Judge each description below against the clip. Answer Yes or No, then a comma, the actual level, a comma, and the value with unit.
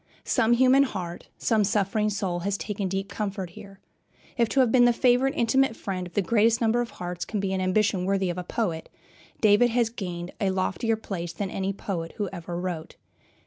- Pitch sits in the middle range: No, high, 200 Hz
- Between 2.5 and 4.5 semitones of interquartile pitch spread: Yes, average, 3.7 semitones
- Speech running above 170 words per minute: Yes, average, 195 wpm